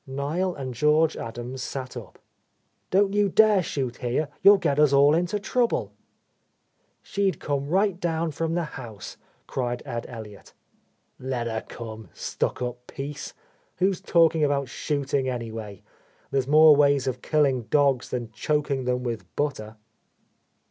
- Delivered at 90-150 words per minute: Yes, average, 140 wpm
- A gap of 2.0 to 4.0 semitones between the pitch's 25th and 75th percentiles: No, average, 4.5 semitones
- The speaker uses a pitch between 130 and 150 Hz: Yes, medium, 140 Hz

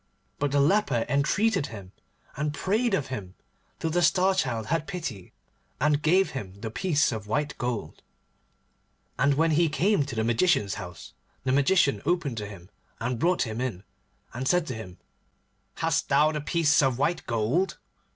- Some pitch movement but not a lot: No, wide, 6.6 semitones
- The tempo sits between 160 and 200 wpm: Yes, average, 170 wpm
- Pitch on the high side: No, medium, 140 Hz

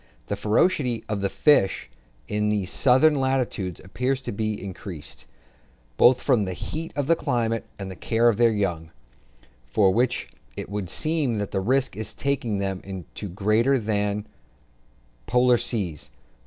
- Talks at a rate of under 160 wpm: No, average, 165 wpm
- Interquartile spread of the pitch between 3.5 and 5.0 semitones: Yes, average, 4.4 semitones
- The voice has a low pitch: Yes, low, 110 Hz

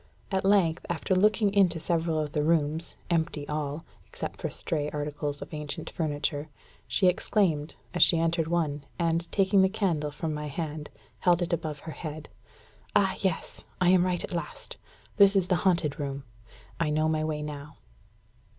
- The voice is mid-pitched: Yes, medium, 160 Hz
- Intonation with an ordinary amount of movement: Yes, average, 3.1 semitones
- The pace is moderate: Yes, average, 170 wpm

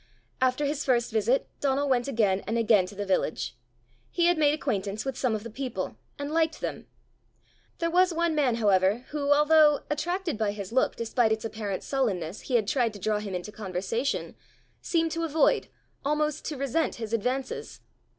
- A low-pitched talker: No, very high, 250 Hz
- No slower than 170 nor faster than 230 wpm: Yes, average, 180 wpm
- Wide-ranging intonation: Yes, wide, 5.8 semitones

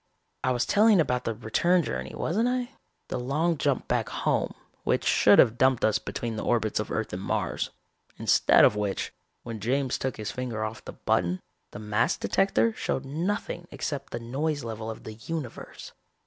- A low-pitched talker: Yes, low, 125 Hz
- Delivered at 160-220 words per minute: Yes, average, 180 wpm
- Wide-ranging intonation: Yes, wide, 6.4 semitones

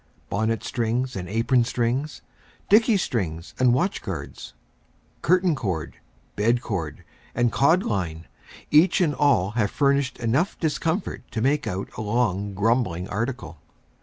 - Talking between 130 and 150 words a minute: Yes, slow, 135 wpm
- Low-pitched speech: Yes, low, 120 Hz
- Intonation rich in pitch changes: Yes, wide, 5.9 semitones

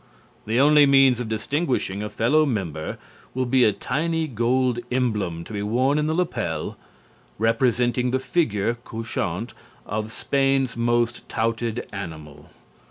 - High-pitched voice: No, low, 120 Hz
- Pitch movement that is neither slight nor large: Yes, average, 3.8 semitones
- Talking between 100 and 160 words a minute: Yes, slow, 135 wpm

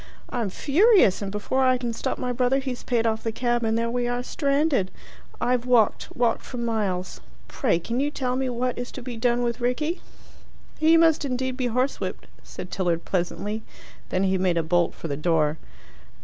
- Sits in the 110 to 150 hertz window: No, high, 240 Hz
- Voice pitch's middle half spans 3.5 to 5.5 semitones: Yes, average, 4.2 semitones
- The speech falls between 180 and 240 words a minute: Yes, average, 190 wpm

